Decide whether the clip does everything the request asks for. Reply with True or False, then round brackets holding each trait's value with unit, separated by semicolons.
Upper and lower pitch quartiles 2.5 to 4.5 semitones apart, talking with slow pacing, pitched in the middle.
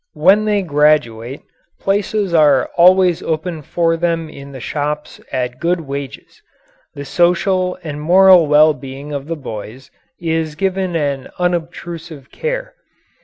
True (4.0 semitones; 130 wpm; 160 Hz)